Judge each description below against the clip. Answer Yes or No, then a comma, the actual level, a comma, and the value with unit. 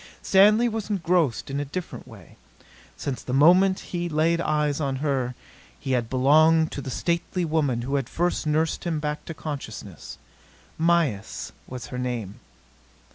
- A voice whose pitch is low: No, medium, 150 Hz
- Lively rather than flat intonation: No, average, 4.7 semitones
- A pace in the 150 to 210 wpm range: Yes, average, 155 wpm